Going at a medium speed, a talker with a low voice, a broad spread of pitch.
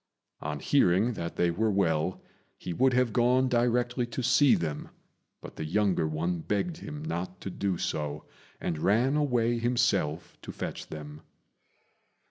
Yes: average, 150 wpm; low, 105 Hz; wide, 6.5 semitones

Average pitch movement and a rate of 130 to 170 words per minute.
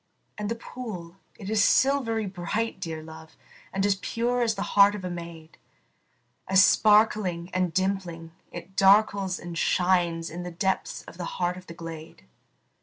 Yes: average, 3.4 semitones; average, 165 wpm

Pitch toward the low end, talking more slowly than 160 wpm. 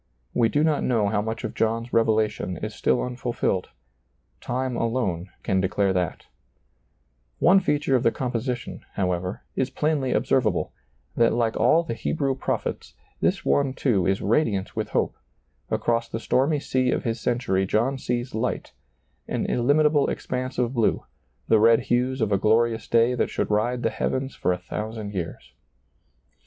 No: low, 115 Hz; average, 165 wpm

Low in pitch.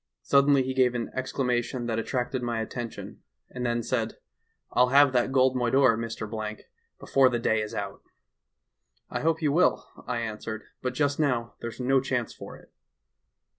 Yes: low, 125 Hz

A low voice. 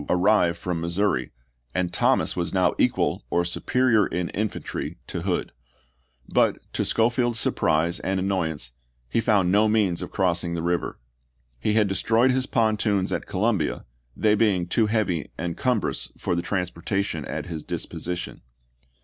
Yes: very low, 95 Hz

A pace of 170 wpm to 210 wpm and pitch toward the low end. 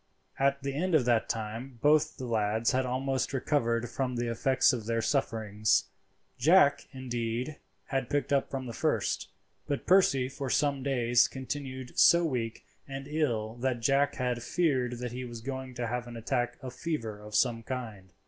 Yes: average, 175 wpm; low, 125 Hz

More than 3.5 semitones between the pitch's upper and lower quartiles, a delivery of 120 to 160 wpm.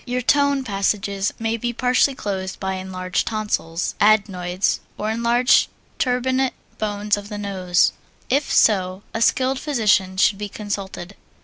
Yes: average, 4.0 semitones; slow, 135 wpm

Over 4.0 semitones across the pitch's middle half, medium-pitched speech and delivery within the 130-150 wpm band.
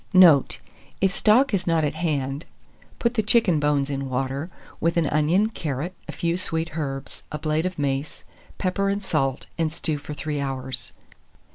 No: average, 4.7 semitones; medium, 155 Hz; average, 170 wpm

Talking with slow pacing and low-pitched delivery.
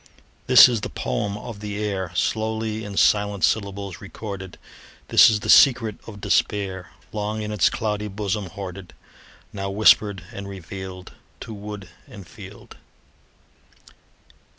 Yes: slow, 130 wpm; low, 100 Hz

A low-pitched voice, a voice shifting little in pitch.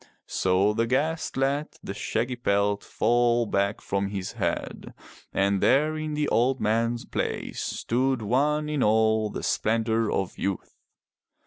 No: low, 115 Hz; average, 4.6 semitones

